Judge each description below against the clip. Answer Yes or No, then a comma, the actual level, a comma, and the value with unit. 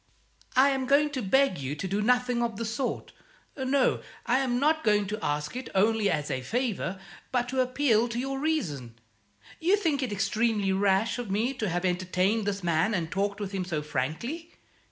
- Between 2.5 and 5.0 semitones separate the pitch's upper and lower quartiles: No, wide, 5.5 semitones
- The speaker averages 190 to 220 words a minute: Yes, average, 195 wpm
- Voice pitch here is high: Yes, high, 220 Hz